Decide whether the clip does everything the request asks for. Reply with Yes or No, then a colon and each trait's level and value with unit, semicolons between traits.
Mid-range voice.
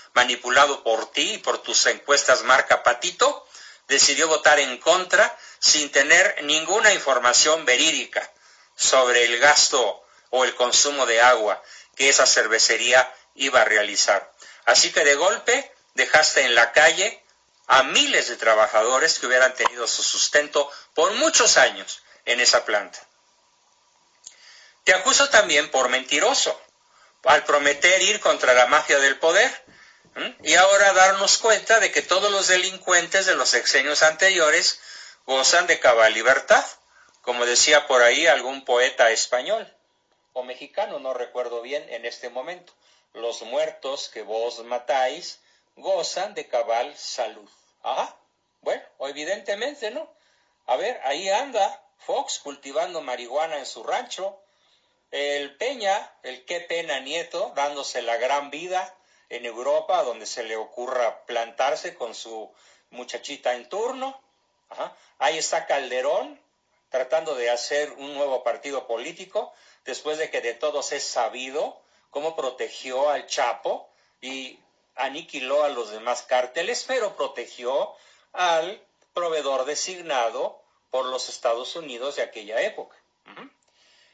Yes: medium, 145 Hz